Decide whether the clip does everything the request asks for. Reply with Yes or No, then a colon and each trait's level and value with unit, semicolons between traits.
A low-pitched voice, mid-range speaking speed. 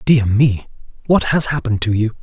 Yes: low, 120 Hz; average, 190 wpm